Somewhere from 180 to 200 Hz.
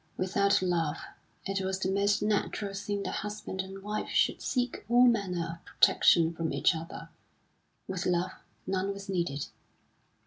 Yes: high, 190 Hz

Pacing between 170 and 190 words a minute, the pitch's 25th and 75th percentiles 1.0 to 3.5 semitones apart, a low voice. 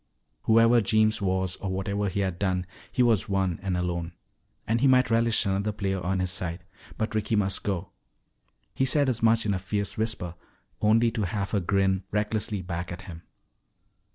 Yes: average, 180 wpm; average, 3.0 semitones; low, 100 Hz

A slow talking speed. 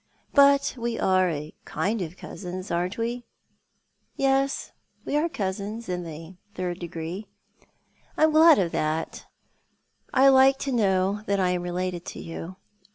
No: average, 160 wpm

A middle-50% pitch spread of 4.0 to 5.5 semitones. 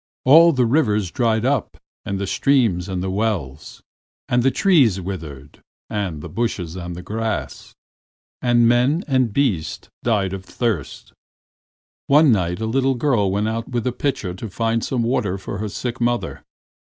Yes: average, 4.7 semitones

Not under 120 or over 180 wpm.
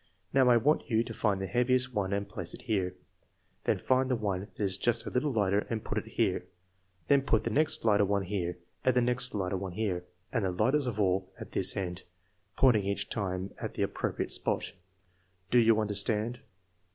No: fast, 205 wpm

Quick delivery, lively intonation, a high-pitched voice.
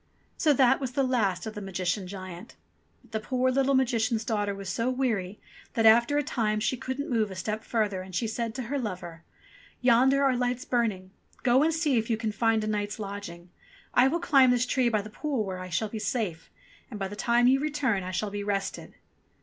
No: fast, 220 wpm; average, 4.1 semitones; high, 225 Hz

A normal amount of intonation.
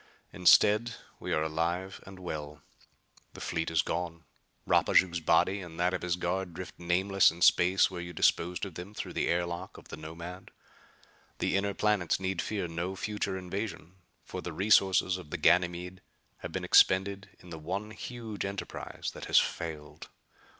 No: narrow, 2.2 semitones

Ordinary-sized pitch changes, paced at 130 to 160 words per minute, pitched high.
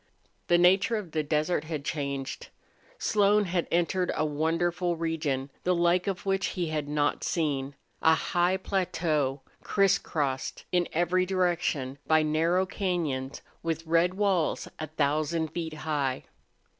No: average, 3.0 semitones; average, 140 wpm; medium, 165 Hz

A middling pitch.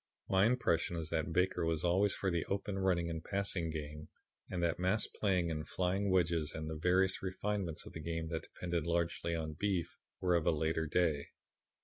No: very low, 85 Hz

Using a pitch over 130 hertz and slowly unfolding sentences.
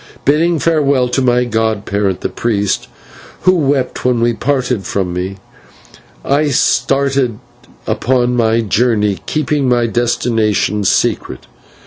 No: low, 120 Hz; slow, 115 wpm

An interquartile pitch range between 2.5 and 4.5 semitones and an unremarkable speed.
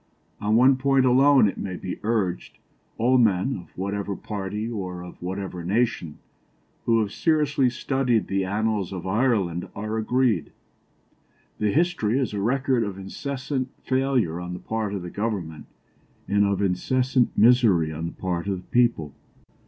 No: average, 5.2 semitones; average, 155 wpm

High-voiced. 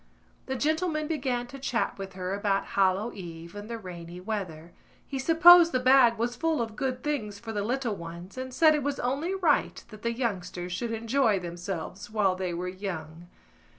Yes: high, 220 Hz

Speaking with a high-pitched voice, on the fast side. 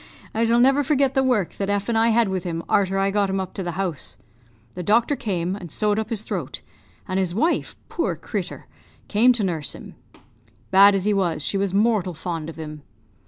Yes: high, 195 Hz; fast, 215 wpm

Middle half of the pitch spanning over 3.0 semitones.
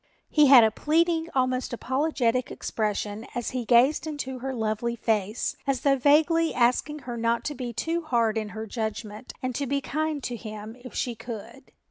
Yes: average, 4.0 semitones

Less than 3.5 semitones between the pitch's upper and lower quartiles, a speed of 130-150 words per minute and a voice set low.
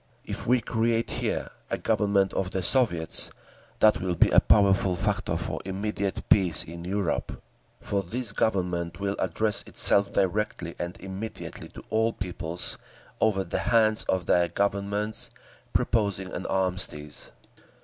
Yes: average, 3.1 semitones; average, 140 wpm; low, 100 Hz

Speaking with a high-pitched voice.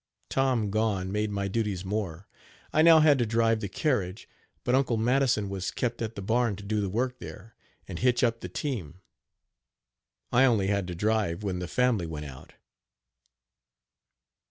No: low, 110 Hz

